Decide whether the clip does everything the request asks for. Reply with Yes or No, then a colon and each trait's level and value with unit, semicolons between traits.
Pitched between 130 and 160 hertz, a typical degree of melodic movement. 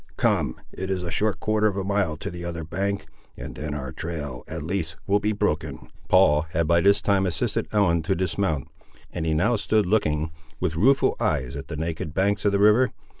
No: very low, 90 Hz; average, 4.2 semitones